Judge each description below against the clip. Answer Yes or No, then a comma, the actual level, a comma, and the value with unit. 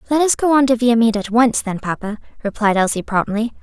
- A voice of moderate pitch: No, high, 230 Hz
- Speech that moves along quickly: Yes, fast, 215 wpm